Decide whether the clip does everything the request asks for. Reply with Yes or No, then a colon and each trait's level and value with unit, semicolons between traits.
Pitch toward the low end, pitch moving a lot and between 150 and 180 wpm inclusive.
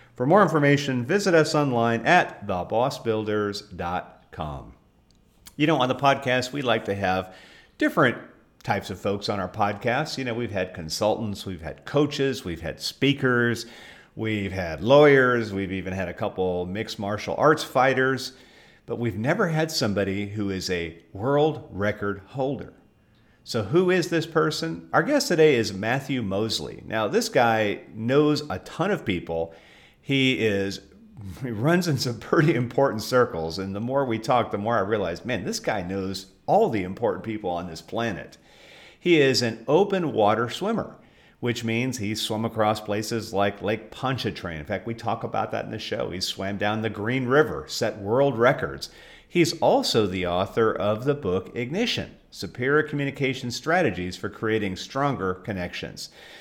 Yes: low, 115 Hz; wide, 5.9 semitones; average, 165 wpm